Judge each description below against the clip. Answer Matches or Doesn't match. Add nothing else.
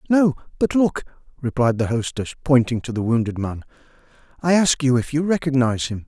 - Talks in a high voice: Doesn't match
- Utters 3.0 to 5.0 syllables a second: Doesn't match